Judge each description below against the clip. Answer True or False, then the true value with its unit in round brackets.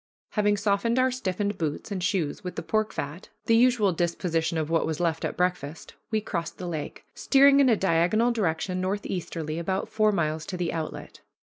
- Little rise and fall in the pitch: False (4.5 semitones)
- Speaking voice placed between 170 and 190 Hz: True (185 Hz)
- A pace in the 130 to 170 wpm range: False (190 wpm)